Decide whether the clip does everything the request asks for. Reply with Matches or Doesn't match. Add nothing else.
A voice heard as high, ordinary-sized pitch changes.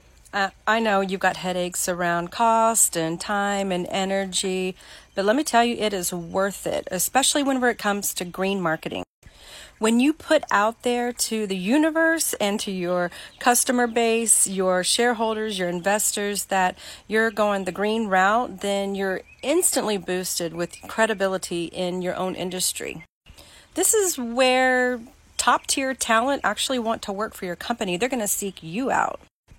Matches